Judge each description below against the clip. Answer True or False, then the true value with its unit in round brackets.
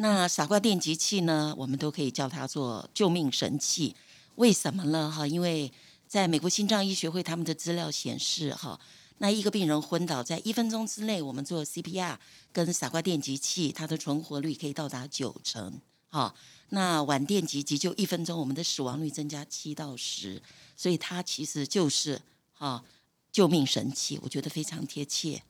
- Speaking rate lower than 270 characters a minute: False (280 characters per minute)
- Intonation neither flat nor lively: True (3.7 semitones)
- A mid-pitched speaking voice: True (155 Hz)